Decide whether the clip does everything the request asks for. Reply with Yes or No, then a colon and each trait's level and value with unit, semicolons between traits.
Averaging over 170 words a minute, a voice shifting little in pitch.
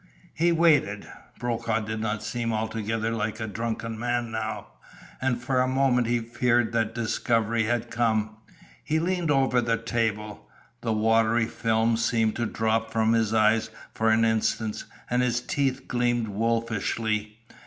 No: average, 150 wpm; narrow, 1.6 semitones